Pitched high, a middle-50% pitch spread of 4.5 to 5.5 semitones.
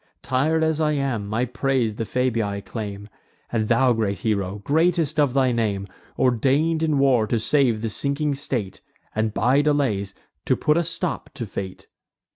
No: low, 125 Hz; average, 5.0 semitones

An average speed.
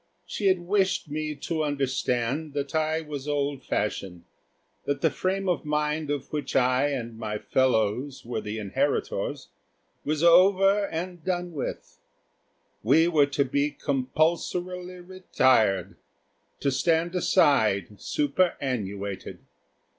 No: slow, 120 wpm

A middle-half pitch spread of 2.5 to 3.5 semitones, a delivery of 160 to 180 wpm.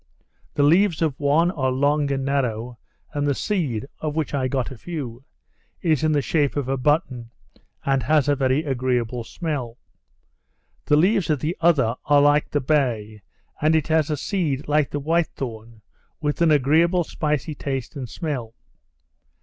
Yes: average, 3.2 semitones; average, 170 wpm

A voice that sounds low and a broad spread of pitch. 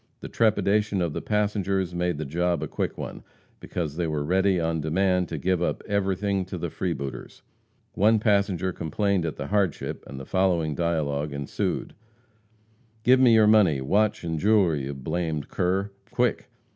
No: very low, 90 Hz; average, 4.0 semitones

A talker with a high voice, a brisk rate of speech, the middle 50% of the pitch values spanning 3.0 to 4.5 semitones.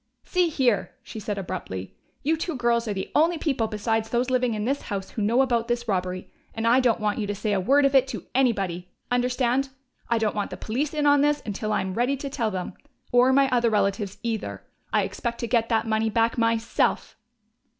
Yes: high, 230 Hz; fast, 220 wpm; average, 3.6 semitones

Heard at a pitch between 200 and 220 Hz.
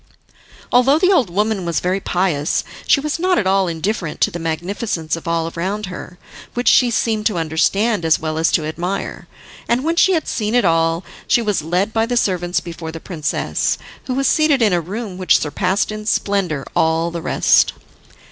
No: high, 190 Hz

